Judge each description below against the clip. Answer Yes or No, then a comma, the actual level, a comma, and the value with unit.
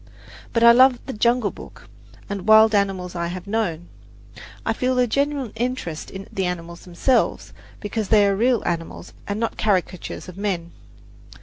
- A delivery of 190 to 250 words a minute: No, average, 165 wpm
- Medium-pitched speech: No, high, 205 Hz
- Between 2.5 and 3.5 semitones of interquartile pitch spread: No, average, 4.5 semitones